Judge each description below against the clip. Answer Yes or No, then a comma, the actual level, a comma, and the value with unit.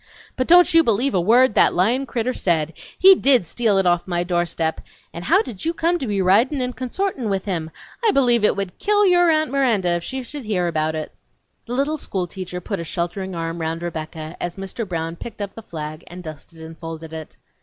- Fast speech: Yes, fast, 220 wpm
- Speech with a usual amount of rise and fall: No, wide, 7.1 semitones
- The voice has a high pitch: Yes, high, 195 Hz